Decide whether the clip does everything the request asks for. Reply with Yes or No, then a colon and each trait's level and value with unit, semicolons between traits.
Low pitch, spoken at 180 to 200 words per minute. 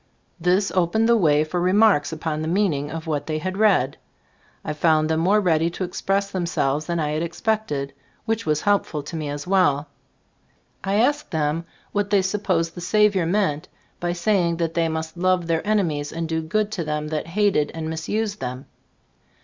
No: medium, 170 Hz; average, 190 wpm